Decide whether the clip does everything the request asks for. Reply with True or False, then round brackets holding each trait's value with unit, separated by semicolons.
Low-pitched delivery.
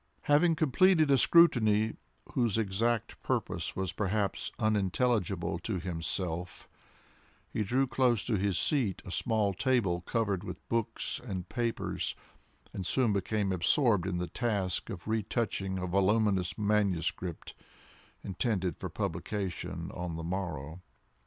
True (100 Hz)